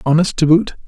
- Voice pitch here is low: No, medium, 155 Hz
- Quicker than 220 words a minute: No, fast, 205 wpm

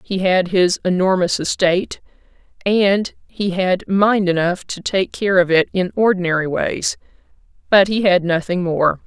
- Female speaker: Yes, female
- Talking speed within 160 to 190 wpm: No, average, 150 wpm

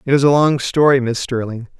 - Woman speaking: No, male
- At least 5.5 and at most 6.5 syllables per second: Yes, 5.6 syllables/s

